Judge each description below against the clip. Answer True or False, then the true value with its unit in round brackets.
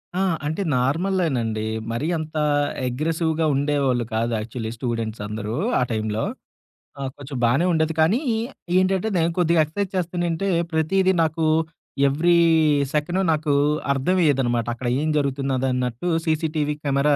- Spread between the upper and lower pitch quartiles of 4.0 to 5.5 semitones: True (4.9 semitones)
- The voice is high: False (150 Hz)